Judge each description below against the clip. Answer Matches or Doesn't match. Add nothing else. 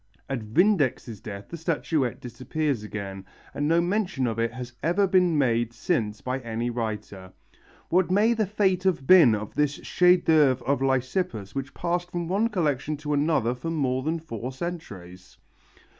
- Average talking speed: Matches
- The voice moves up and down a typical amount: Doesn't match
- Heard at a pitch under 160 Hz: Matches